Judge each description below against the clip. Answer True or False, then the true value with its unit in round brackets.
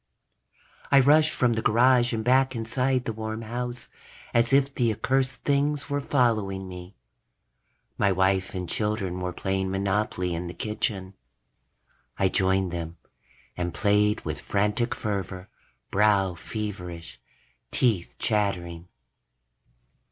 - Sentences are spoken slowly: True (125 wpm)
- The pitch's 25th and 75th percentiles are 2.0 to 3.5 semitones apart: False (4.4 semitones)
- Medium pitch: False (105 Hz)